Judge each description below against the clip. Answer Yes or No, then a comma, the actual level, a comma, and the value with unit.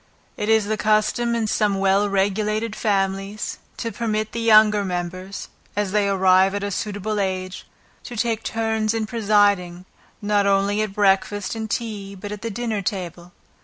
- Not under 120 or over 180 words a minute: Yes, average, 165 wpm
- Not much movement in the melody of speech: Yes, narrow, 1.9 semitones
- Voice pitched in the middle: No, high, 205 Hz